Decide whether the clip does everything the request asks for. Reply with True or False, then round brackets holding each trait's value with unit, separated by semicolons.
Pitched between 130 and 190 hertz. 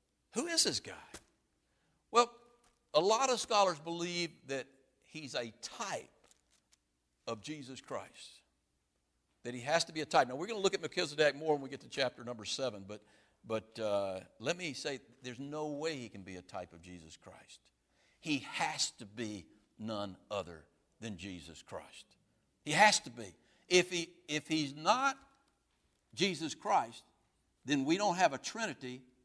True (135 Hz)